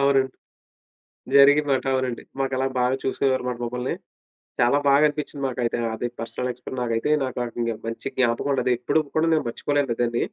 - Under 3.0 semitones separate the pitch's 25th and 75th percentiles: Yes, narrow, 2.4 semitones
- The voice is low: Yes, low, 130 Hz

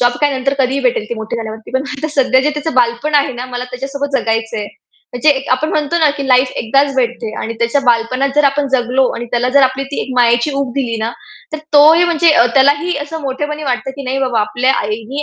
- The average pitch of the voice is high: Yes, very high, 265 Hz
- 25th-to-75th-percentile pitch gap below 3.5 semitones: Yes, average, 3.0 semitones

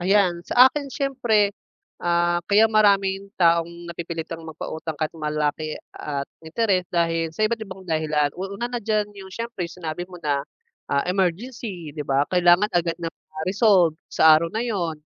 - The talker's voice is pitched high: No, medium, 175 Hz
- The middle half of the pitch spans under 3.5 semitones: No, average, 4.2 semitones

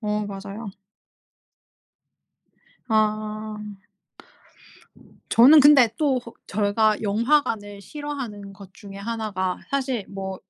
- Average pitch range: Yes, average, 3.5 semitones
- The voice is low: No, high, 215 Hz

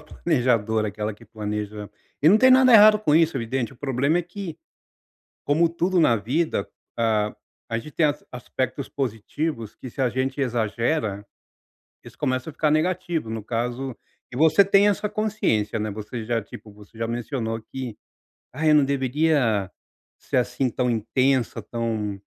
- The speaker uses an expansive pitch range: Yes, wide, 5.7 semitones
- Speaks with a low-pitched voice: Yes, low, 125 Hz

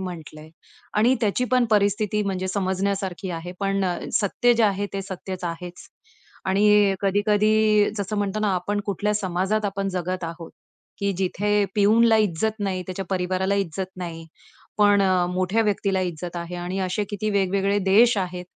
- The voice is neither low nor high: No, high, 195 Hz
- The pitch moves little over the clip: Yes, narrow, 2.2 semitones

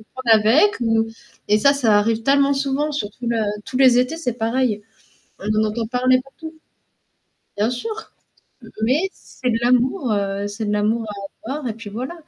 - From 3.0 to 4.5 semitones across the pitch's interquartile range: Yes, average, 3.8 semitones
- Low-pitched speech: No, high, 245 Hz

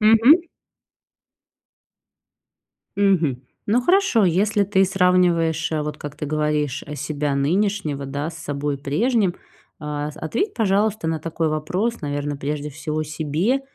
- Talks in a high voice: No, medium, 160 Hz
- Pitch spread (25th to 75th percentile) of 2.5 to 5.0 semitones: No, wide, 5.4 semitones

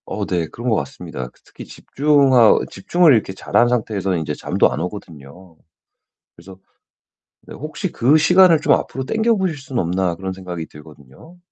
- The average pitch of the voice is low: Yes, low, 105 Hz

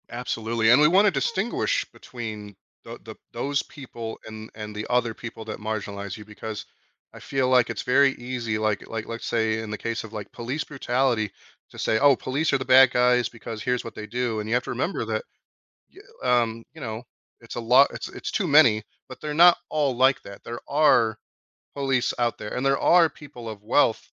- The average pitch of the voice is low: Yes, low, 120 Hz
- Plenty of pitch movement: No, average, 3.3 semitones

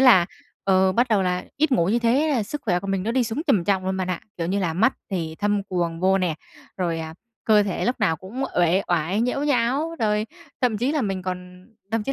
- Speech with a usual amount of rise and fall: Yes, average, 4.7 semitones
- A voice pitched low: No, high, 195 Hz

